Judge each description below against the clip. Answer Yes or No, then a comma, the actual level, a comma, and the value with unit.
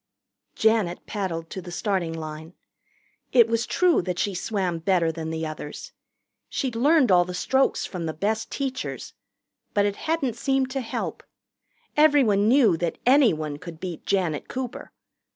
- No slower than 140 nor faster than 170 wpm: Yes, average, 150 wpm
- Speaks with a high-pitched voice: Yes, high, 195 Hz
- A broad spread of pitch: Yes, wide, 7.0 semitones